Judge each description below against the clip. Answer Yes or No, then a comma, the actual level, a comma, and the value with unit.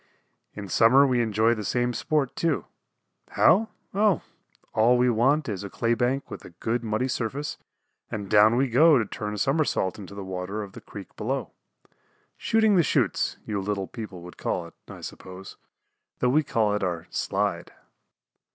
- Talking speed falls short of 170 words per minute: No, average, 175 wpm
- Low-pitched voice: Yes, low, 115 Hz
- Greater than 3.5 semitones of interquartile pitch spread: Yes, average, 4.7 semitones